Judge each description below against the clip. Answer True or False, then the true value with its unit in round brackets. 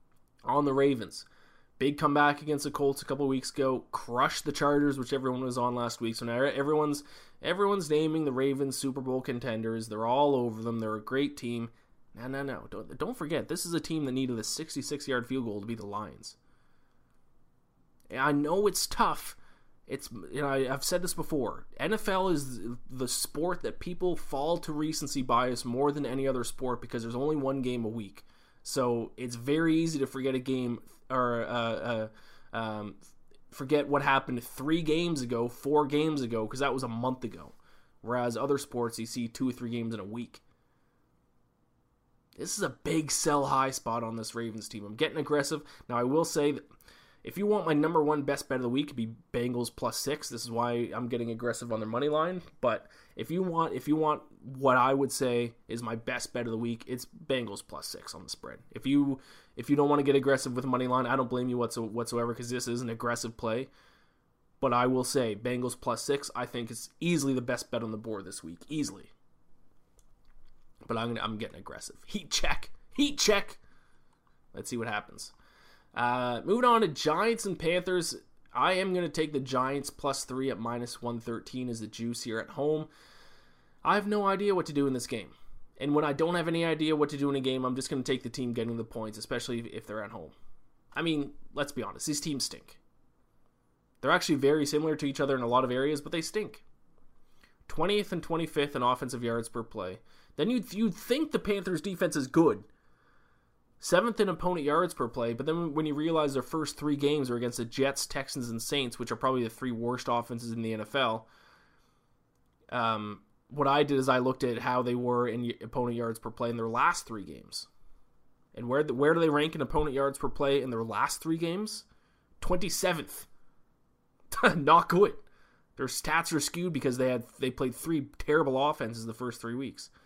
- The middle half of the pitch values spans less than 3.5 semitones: False (4.0 semitones)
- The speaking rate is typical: False (210 wpm)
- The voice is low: True (130 Hz)